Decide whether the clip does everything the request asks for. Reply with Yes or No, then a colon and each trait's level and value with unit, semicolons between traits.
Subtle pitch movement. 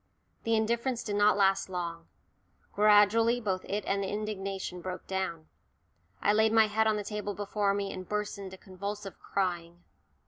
Yes: narrow, 1.9 semitones